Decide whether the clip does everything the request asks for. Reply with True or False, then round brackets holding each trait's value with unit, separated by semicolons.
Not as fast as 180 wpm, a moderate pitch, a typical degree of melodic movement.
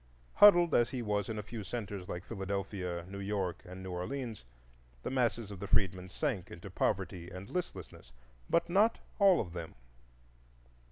False (165 wpm; 100 Hz; 4.8 semitones)